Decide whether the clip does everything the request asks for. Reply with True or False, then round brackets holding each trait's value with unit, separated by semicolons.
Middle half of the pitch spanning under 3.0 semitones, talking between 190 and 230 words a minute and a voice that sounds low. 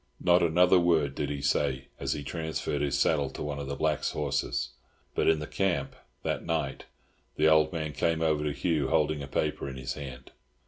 True (2.4 semitones; 200 wpm; 75 Hz)